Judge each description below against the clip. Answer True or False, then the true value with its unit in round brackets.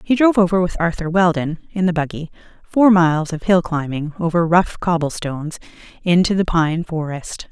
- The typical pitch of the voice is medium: True (170 Hz)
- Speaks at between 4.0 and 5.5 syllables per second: True (5.2 syllables/s)